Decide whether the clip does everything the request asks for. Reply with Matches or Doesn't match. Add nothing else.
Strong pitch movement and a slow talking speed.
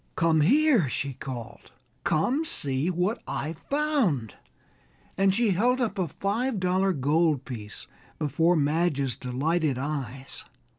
Matches